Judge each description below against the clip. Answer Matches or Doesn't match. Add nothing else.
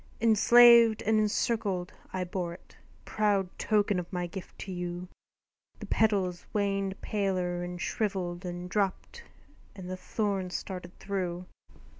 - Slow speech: Matches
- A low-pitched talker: Doesn't match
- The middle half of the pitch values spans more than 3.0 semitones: Doesn't match